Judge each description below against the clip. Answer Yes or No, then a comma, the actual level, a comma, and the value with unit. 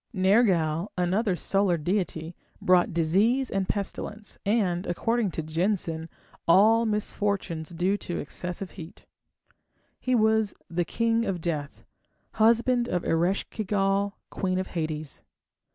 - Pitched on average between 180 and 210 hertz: Yes, high, 190 Hz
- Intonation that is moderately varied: Yes, average, 3.9 semitones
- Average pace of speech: No, slow, 120 wpm